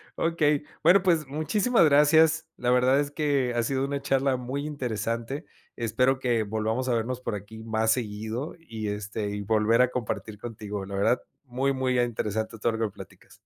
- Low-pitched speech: Yes, low, 125 Hz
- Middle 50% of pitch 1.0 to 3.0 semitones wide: No, average, 4.2 semitones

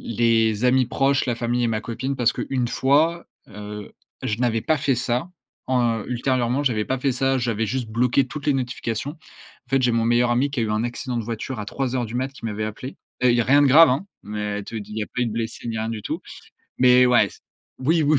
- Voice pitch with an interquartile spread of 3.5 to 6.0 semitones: No, average, 2.8 semitones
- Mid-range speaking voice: No, low, 120 Hz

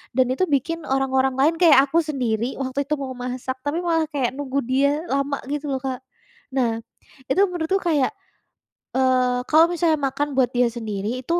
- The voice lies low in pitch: No, very high, 270 Hz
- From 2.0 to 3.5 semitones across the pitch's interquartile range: Yes, average, 2.9 semitones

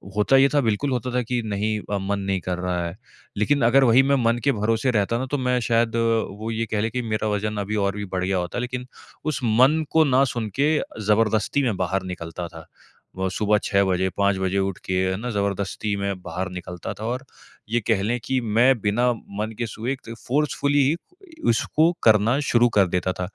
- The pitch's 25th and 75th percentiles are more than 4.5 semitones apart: No, average, 4.0 semitones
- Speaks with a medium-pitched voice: No, low, 110 Hz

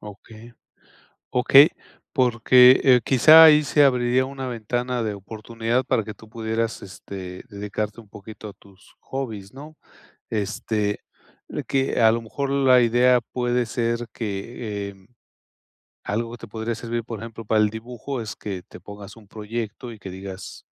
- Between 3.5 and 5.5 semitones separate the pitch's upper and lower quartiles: No, average, 3.0 semitones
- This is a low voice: Yes, low, 115 Hz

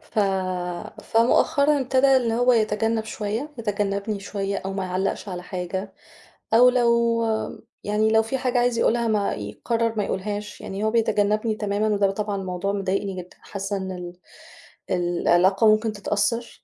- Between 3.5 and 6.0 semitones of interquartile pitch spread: No, average, 2.9 semitones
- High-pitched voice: Yes, high, 210 Hz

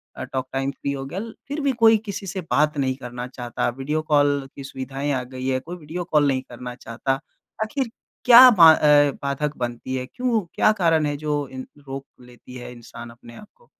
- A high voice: No, medium, 140 Hz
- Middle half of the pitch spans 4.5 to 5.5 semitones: No, average, 3.7 semitones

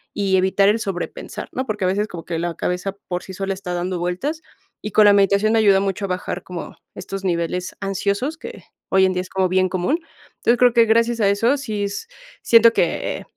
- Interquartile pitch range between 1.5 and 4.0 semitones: Yes, average, 2.8 semitones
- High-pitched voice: Yes, high, 195 Hz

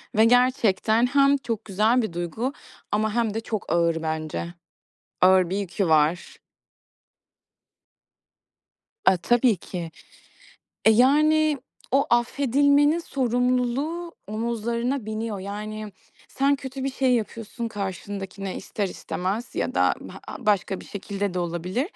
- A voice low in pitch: No, high, 220 Hz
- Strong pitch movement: No, average, 4.8 semitones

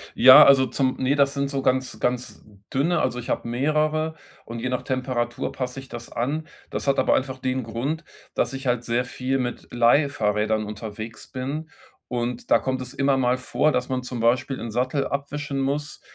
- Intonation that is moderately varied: No, narrow, 2.3 semitones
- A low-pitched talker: Yes, low, 130 Hz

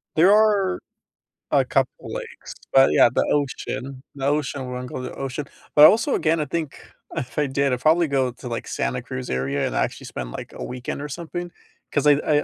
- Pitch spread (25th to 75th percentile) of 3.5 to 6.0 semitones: Yes, average, 4.0 semitones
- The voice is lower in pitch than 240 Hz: Yes, medium, 140 Hz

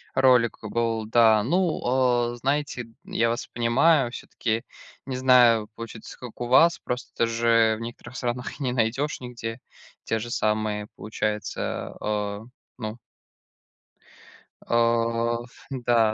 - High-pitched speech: No, low, 120 Hz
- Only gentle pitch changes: Yes, narrow, 2.1 semitones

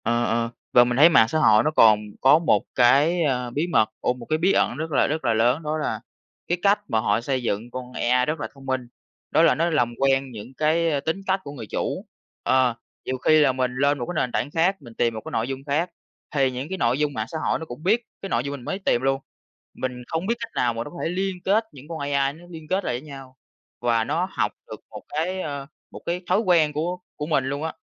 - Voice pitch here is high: No, medium, 140 Hz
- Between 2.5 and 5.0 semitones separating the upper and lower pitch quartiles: Yes, average, 4.7 semitones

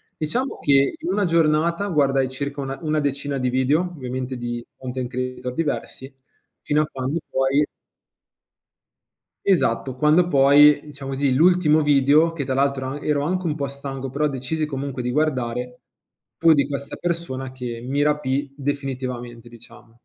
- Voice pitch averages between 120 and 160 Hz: Yes, medium, 140 Hz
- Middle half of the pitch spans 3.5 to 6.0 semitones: No, average, 2.7 semitones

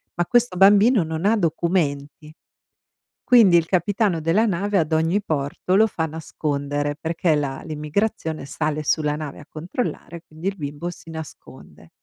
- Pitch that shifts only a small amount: No, average, 4.1 semitones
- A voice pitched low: No, medium, 165 Hz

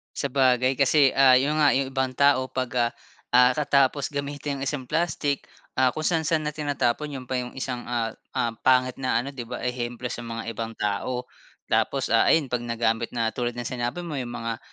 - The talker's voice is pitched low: Yes, low, 130 Hz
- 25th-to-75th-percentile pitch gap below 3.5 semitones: Yes, narrow, 2.6 semitones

